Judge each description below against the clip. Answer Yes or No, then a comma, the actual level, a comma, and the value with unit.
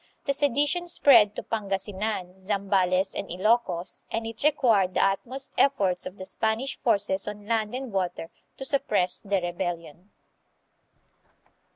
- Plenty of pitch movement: No, average, 4.1 semitones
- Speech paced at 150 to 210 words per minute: No, average, 140 wpm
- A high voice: Yes, high, 205 Hz